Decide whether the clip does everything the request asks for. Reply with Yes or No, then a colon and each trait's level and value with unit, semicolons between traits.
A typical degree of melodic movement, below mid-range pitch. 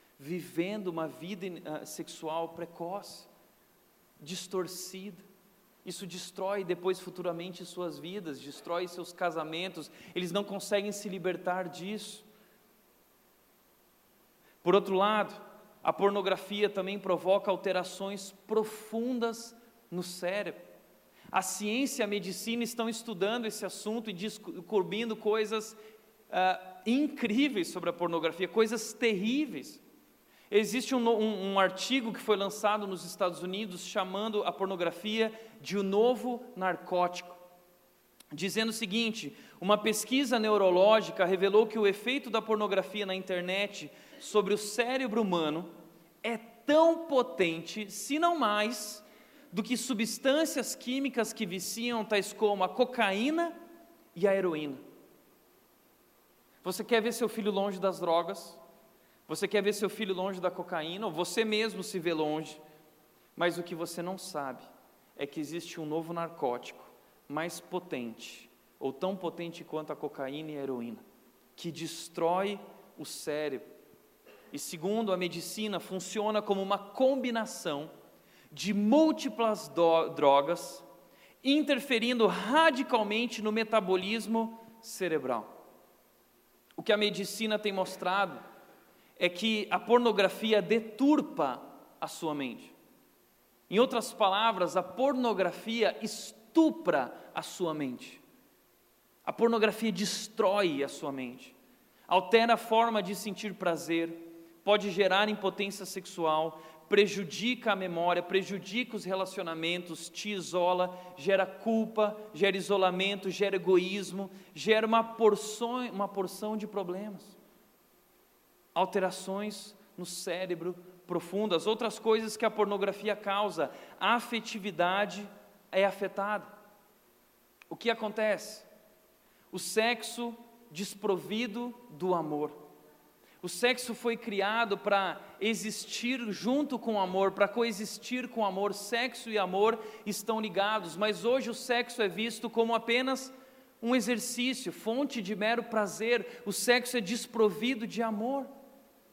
No: average, 3.8 semitones; high, 205 Hz